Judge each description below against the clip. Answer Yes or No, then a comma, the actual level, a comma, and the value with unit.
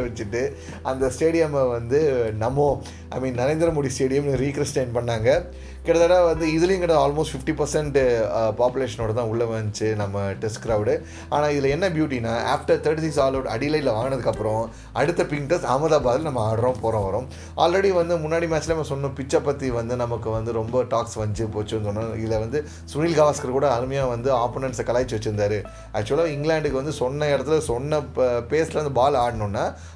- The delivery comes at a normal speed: No, fast, 160 wpm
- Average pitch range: Yes, average, 5.0 semitones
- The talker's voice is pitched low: Yes, low, 130 Hz